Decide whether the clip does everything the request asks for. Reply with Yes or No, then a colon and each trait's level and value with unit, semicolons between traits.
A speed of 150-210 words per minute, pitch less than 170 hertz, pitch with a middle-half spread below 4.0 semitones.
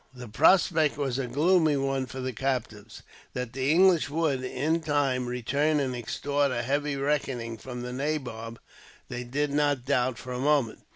Yes: average, 170 wpm; low, 135 Hz; average, 2.9 semitones